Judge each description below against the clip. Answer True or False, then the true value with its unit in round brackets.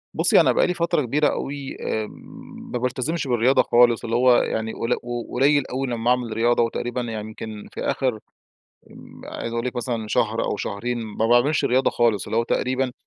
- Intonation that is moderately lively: False (2.2 semitones)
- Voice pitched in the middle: False (120 Hz)